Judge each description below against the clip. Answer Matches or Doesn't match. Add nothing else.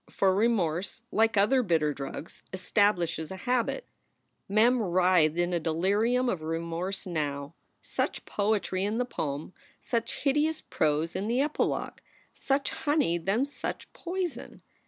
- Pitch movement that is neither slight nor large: Doesn't match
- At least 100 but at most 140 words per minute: Matches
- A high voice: Matches